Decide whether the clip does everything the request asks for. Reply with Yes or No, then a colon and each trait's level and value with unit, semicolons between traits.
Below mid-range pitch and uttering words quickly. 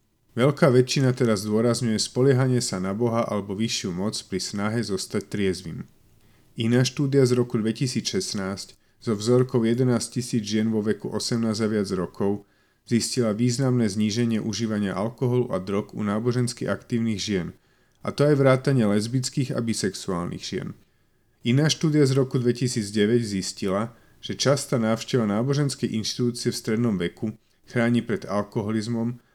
No: low, 115 Hz; average, 140 wpm